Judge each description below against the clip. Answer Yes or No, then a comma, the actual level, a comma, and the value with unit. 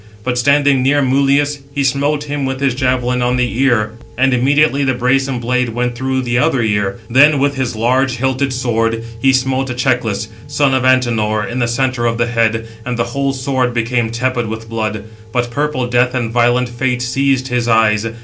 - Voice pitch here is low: Yes, low, 125 Hz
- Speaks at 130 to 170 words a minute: No, average, 190 wpm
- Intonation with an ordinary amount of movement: No, narrow, 2.2 semitones